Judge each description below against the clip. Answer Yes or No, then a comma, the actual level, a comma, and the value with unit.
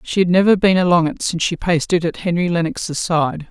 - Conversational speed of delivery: No, fast, 240 wpm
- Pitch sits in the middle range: Yes, medium, 170 Hz